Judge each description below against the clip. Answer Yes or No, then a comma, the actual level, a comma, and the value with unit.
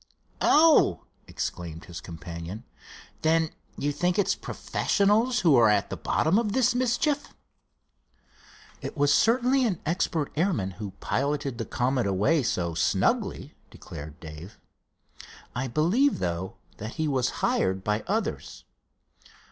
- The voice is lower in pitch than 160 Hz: Yes, medium, 140 Hz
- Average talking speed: No, slow, 125 wpm